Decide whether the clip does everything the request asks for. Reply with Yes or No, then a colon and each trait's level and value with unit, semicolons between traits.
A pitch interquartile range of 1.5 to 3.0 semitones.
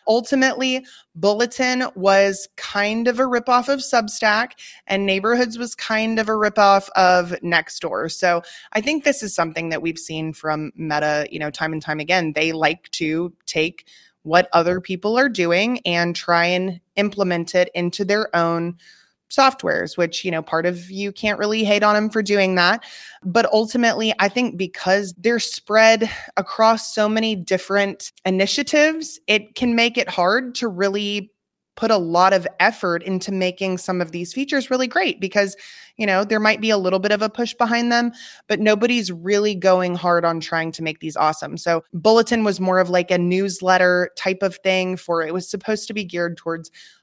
No: average, 4.0 semitones